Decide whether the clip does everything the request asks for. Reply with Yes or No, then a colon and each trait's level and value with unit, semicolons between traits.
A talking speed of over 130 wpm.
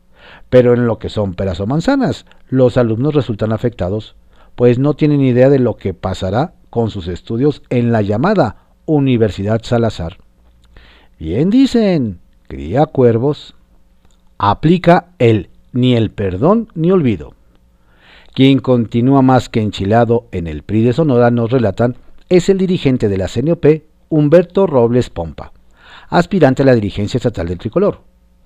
Yes: average, 140 wpm